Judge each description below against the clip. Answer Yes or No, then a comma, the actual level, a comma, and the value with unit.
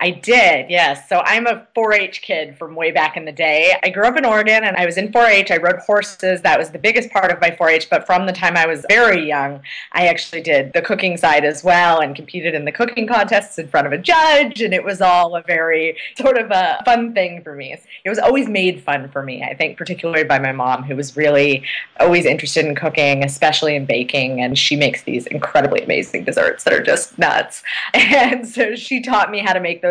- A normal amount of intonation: No, wide, 6.0 semitones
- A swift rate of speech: Yes, fast, 245 wpm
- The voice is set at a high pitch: No, medium, 175 Hz